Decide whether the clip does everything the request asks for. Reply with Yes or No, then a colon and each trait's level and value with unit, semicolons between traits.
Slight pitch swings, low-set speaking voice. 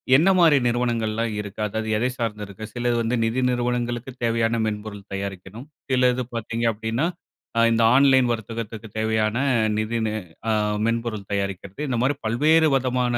Yes: narrow, 2.3 semitones; low, 115 Hz